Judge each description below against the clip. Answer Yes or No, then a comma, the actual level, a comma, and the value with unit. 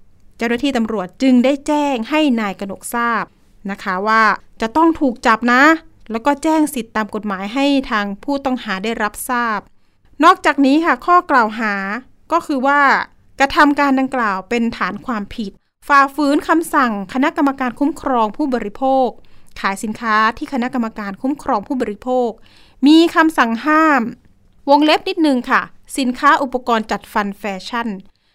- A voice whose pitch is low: No, very high, 250 Hz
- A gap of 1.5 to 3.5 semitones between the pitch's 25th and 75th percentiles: No, average, 4.8 semitones